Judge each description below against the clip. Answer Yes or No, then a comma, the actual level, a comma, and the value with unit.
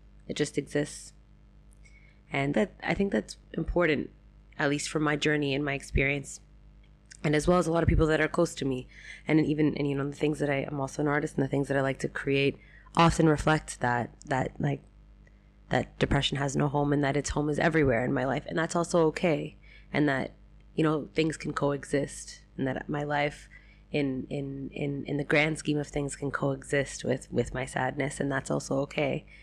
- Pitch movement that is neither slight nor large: No, narrow, 1.9 semitones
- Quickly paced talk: Yes, fast, 210 wpm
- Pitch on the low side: No, medium, 145 Hz